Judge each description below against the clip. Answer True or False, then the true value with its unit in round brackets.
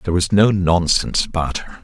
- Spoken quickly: False (195 wpm)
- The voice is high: False (90 Hz)